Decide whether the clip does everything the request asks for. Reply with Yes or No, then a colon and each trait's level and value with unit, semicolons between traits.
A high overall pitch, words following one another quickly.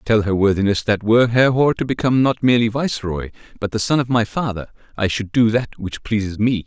No: low, 110 Hz; fast, 215 wpm